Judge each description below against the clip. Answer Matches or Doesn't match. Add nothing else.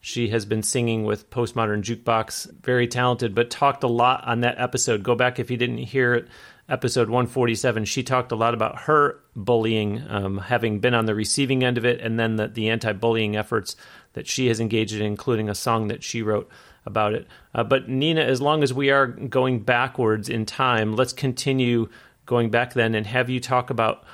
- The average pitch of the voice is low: Matches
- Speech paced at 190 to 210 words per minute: Matches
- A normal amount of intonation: Doesn't match